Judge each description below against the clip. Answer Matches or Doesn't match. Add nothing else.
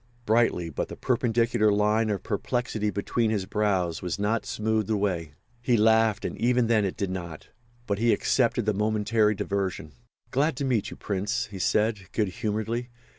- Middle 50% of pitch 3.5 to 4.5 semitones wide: Doesn't match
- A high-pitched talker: Doesn't match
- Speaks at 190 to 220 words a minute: Doesn't match